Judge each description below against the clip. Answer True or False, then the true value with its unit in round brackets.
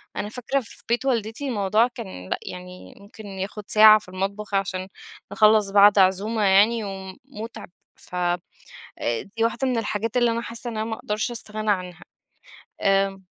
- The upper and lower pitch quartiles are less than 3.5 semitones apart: True (2.8 semitones)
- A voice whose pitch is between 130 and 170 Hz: False (210 Hz)